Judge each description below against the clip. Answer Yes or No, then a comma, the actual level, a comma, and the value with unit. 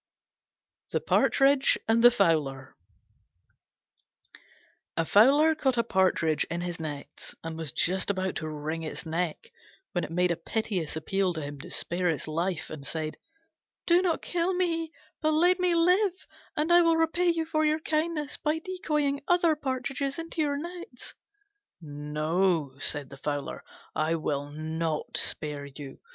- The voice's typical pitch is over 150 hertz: Yes, high, 190 Hz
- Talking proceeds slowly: No, average, 155 wpm